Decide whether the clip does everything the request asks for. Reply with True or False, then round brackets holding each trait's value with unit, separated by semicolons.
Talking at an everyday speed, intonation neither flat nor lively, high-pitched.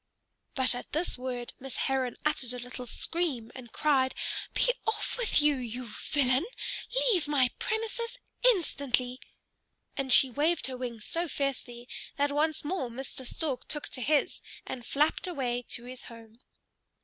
True (150 wpm; 3.4 semitones; 265 Hz)